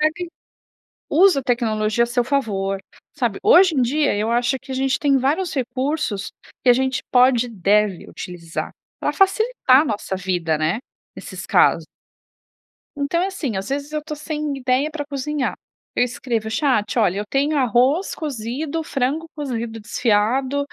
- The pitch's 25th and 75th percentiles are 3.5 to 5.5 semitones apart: Yes, average, 5.0 semitones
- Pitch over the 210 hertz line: Yes, very high, 260 Hz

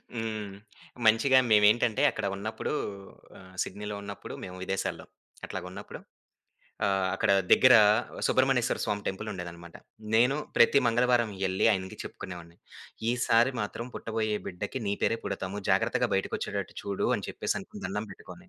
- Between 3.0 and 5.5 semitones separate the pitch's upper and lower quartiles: Yes, average, 3.4 semitones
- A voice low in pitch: Yes, low, 105 Hz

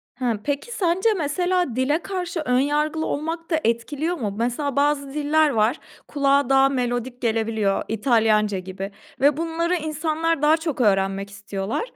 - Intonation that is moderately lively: No, wide, 5.8 semitones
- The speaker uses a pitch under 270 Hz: No, very high, 280 Hz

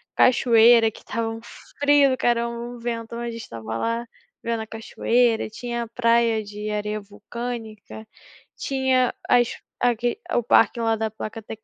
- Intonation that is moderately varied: No, narrow, 1.5 semitones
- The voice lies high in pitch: Yes, high, 230 Hz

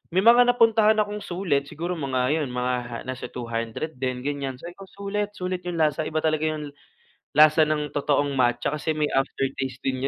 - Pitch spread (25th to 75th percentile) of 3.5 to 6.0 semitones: Yes, average, 5.0 semitones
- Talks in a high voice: No, medium, 150 Hz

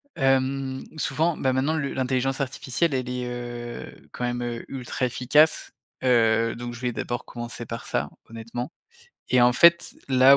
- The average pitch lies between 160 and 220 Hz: No, low, 125 Hz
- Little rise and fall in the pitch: Yes, narrow, 1.8 semitones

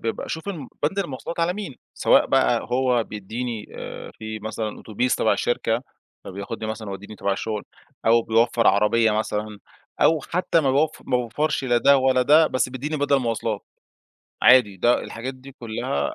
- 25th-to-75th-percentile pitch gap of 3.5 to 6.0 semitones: Yes, average, 4.1 semitones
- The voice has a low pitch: Yes, low, 120 Hz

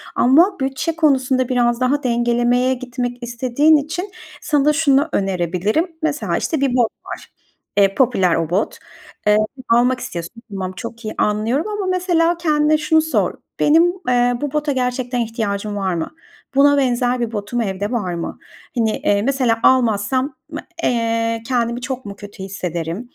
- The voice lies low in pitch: No, high, 245 Hz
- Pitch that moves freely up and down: No, average, 4.9 semitones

